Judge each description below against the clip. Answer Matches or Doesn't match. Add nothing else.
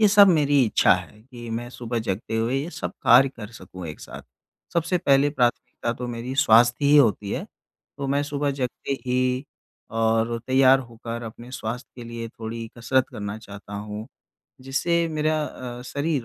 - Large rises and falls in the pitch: Doesn't match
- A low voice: Matches